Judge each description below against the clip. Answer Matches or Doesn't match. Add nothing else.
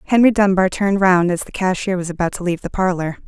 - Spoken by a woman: Matches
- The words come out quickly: Matches